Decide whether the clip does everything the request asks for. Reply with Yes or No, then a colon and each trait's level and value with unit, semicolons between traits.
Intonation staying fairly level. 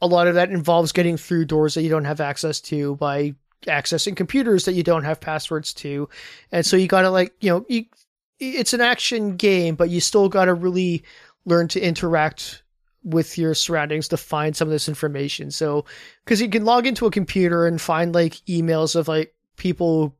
No: average, 3.1 semitones